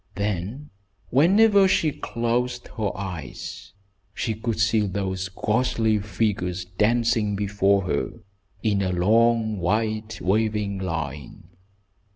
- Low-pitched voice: Yes, low, 105 Hz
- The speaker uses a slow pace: Yes, slow, 105 wpm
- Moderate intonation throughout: Yes, average, 3.4 semitones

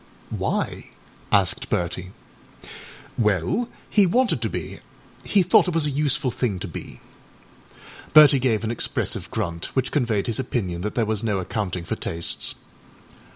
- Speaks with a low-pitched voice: Yes, low, 110 Hz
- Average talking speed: Yes, average, 155 wpm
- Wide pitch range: Yes, wide, 7.6 semitones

